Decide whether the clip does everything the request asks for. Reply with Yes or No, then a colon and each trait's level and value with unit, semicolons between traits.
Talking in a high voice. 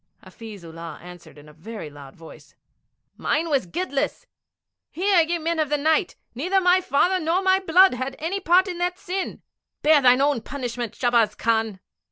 Yes: very high, 290 Hz